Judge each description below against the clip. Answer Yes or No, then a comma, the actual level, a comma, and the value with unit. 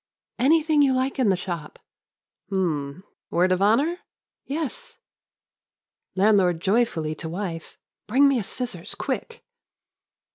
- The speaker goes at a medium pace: No, slow, 115 wpm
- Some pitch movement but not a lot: No, wide, 7.4 semitones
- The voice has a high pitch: Yes, high, 205 Hz